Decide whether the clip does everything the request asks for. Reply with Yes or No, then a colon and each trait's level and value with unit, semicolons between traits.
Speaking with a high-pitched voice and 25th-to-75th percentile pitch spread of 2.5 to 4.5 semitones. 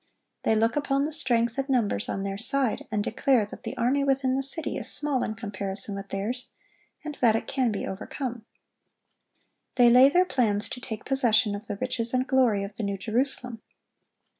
Yes: high, 235 Hz; average, 4.0 semitones